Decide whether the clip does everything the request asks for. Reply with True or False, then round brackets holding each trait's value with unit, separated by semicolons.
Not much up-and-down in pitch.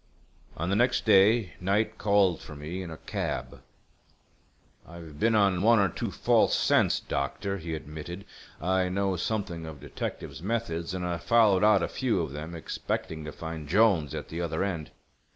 False (3.9 semitones)